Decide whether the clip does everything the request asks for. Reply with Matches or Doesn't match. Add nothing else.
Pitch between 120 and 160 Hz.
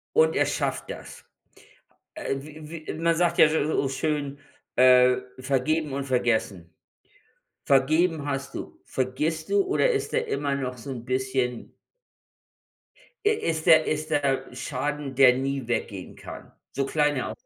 Matches